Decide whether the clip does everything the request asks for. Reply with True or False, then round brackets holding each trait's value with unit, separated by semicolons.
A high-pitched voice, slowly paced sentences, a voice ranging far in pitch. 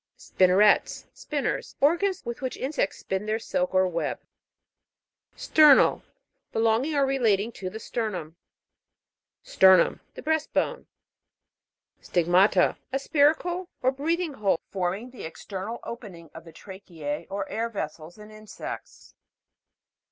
True (215 Hz; 120 wpm; 6.6 semitones)